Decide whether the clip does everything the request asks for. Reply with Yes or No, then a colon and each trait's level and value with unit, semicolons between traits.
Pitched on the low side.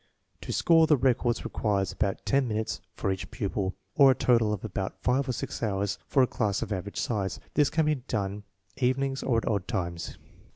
Yes: low, 110 Hz